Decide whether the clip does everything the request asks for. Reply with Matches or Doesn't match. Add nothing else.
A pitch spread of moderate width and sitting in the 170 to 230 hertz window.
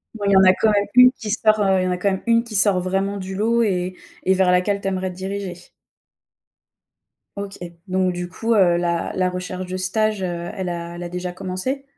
Doesn't match